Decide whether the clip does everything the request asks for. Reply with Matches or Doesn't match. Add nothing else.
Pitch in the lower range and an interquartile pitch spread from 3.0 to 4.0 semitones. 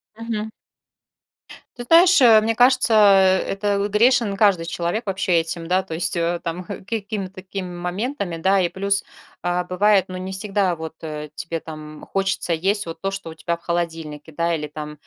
Doesn't match